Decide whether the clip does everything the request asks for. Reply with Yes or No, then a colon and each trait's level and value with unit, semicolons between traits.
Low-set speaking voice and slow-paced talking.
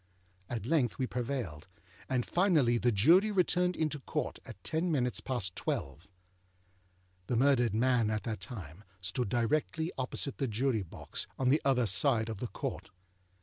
No: low, 125 Hz; average, 155 wpm